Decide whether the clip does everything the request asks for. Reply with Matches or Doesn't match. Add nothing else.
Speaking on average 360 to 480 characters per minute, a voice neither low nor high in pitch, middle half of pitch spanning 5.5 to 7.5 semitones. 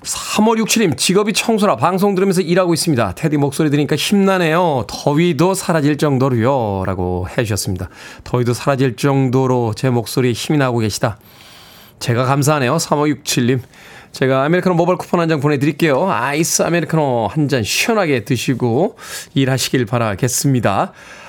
Matches